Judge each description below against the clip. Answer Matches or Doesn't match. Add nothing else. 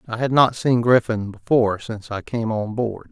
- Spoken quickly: Matches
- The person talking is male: Matches